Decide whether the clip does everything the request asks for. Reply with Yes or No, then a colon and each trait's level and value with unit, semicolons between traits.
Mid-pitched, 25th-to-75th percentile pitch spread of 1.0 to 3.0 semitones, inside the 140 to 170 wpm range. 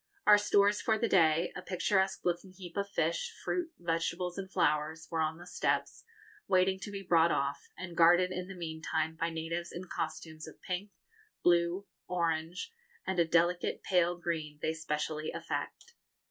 Yes: medium, 175 Hz; narrow, 2.6 semitones; average, 165 wpm